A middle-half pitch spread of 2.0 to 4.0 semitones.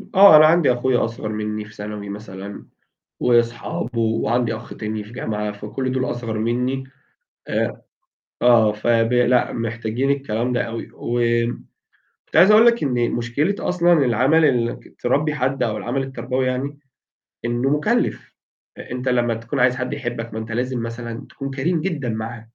Yes: average, 2.8 semitones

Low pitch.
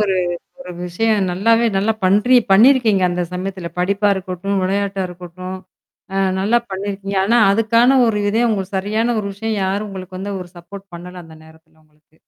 No: high, 195 Hz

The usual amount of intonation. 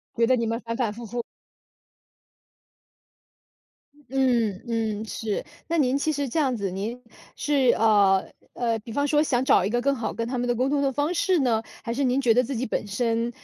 Yes: average, 3.1 semitones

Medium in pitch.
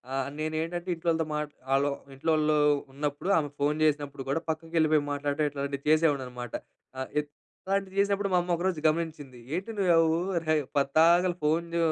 Yes: medium, 155 Hz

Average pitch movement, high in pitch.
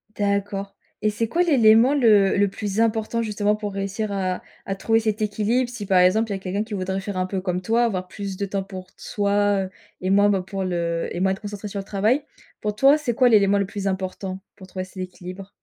No: narrow, 2.2 semitones; high, 200 Hz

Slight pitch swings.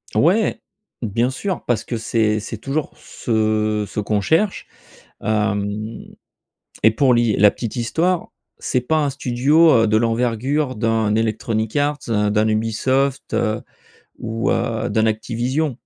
No: average, 3.6 semitones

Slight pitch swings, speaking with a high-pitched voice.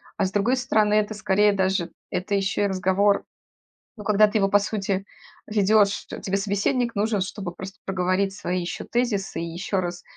Yes: narrow, 1.7 semitones; high, 200 Hz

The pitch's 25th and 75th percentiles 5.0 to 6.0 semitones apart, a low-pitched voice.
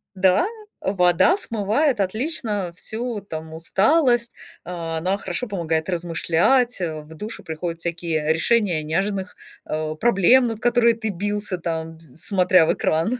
No: wide, 5.4 semitones; medium, 185 Hz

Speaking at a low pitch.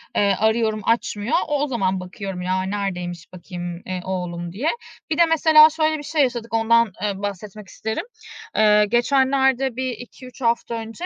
No: high, 220 Hz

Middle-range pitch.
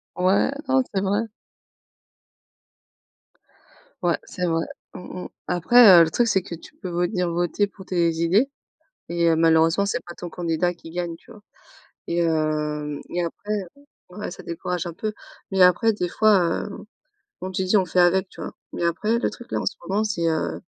Yes: medium, 180 Hz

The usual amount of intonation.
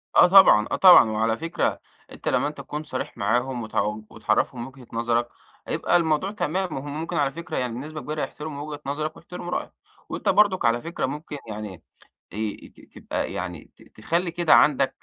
No: wide, 5.8 semitones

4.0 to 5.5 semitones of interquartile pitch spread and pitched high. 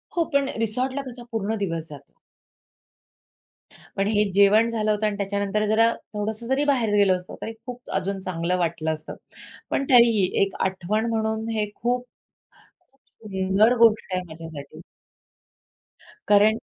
No: average, 3.3 semitones; high, 210 Hz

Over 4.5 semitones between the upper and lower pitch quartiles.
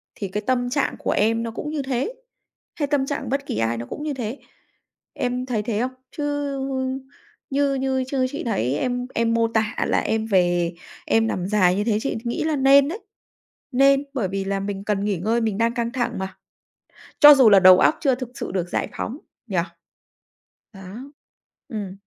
Yes: average, 5.0 semitones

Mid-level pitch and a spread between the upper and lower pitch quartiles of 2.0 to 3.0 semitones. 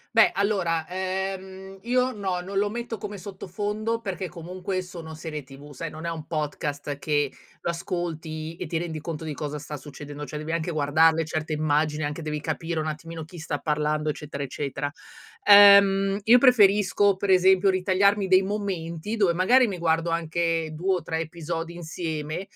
No: medium, 170 Hz; average, 3.7 semitones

